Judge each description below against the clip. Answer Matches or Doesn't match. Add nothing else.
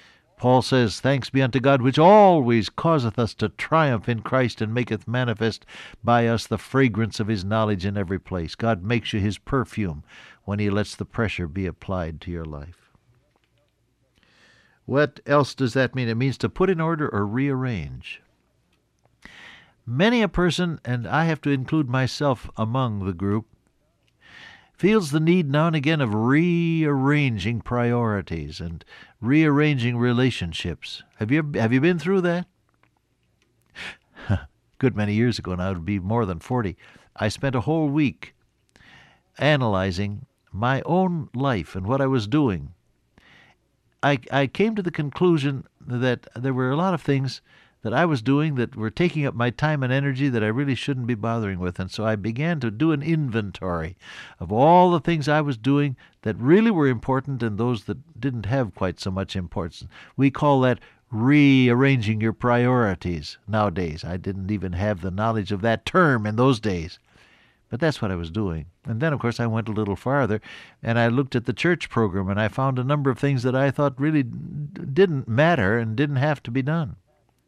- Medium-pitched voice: Doesn't match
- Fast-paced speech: Doesn't match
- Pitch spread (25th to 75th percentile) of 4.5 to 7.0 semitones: Matches